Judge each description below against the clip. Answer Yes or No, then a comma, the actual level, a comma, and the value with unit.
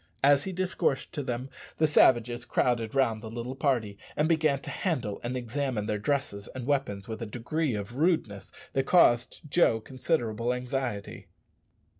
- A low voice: Yes, low, 125 Hz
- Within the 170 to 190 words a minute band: No, average, 160 wpm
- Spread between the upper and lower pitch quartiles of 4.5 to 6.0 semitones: No, average, 4.1 semitones